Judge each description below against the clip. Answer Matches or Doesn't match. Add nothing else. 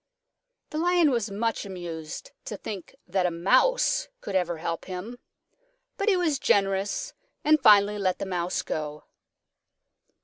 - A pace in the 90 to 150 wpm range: Matches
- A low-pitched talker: Doesn't match